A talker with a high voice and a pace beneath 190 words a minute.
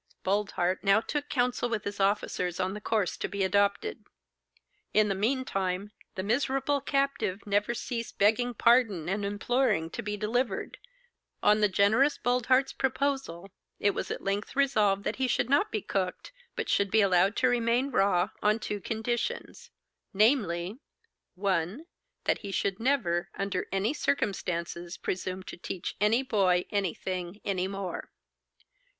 Yes: high, 205 Hz; average, 150 wpm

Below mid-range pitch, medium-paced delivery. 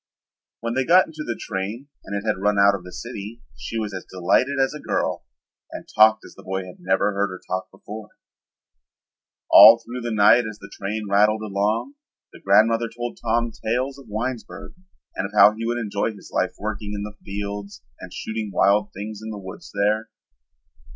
Yes: low, 105 Hz; average, 195 wpm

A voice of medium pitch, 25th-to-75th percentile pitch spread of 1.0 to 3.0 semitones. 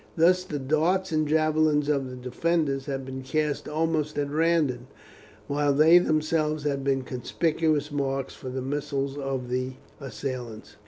Yes: medium, 145 Hz; average, 2.7 semitones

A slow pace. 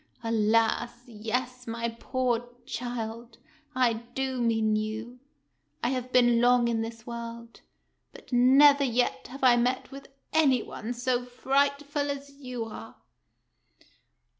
Yes: slow, 125 wpm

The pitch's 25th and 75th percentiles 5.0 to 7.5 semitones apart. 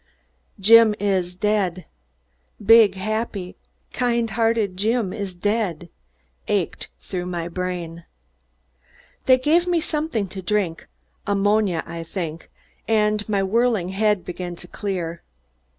No: average, 3.8 semitones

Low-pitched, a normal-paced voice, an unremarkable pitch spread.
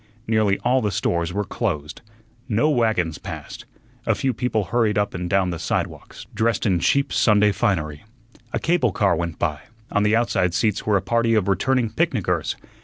Yes: low, 105 Hz; average, 180 wpm; average, 4.5 semitones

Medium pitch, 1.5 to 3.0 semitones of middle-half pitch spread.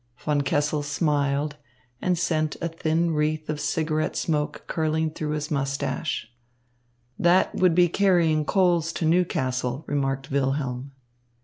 Yes: medium, 155 Hz; narrow, 2.4 semitones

